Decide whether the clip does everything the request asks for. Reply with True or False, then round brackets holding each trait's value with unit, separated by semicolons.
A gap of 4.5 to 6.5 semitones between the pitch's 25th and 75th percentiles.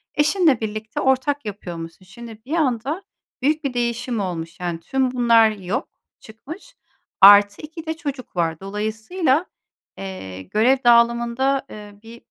True (5.0 semitones)